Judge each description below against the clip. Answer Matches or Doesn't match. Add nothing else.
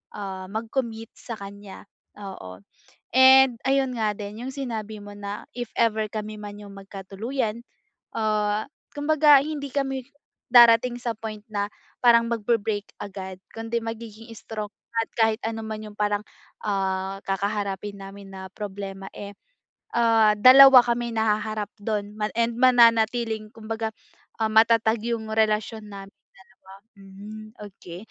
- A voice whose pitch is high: Matches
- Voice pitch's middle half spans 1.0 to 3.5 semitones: Matches